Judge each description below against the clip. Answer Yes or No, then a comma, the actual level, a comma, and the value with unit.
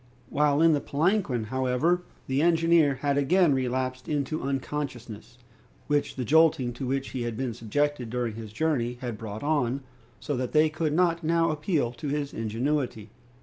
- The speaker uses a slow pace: No, average, 165 wpm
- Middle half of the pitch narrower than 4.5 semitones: Yes, average, 4.1 semitones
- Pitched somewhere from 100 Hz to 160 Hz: Yes, medium, 140 Hz